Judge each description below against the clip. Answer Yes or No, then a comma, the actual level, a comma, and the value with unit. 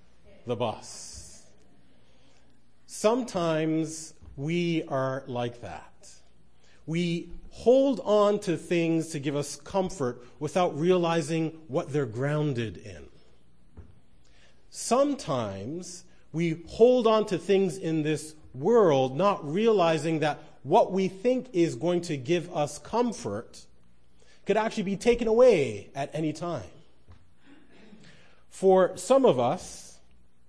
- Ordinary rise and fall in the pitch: No, wide, 6.0 semitones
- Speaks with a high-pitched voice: No, medium, 160 Hz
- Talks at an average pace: No, slow, 110 wpm